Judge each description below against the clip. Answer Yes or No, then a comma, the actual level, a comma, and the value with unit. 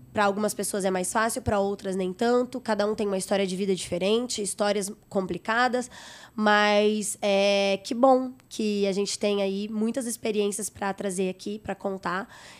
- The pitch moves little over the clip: Yes, narrow, 1.8 semitones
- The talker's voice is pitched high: Yes, high, 205 Hz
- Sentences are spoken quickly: No, average, 170 wpm